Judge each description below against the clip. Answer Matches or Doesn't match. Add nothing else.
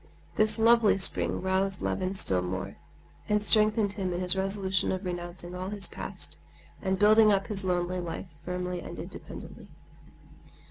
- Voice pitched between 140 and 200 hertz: Matches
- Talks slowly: Doesn't match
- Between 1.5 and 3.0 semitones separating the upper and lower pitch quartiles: Matches